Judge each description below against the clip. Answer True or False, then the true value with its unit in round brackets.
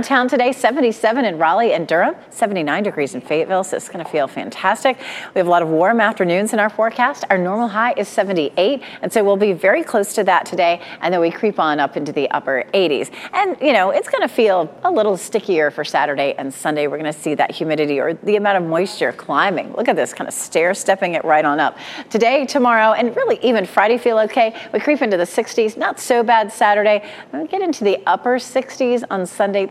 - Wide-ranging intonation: True (5.7 semitones)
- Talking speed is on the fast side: True (230 wpm)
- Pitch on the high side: True (215 Hz)